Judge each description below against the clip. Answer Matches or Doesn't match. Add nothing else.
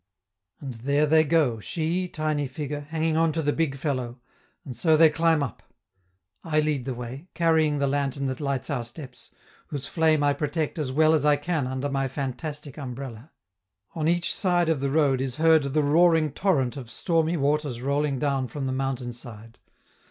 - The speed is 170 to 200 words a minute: Matches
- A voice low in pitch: Doesn't match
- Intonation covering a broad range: Doesn't match